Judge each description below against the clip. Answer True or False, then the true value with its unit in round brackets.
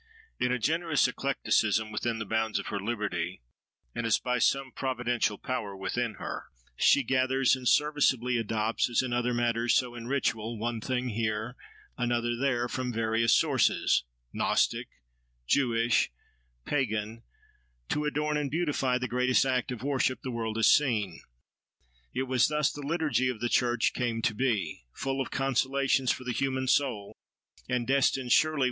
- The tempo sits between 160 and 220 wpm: False (150 wpm)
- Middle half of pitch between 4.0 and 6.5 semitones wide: False (2.8 semitones)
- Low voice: True (125 Hz)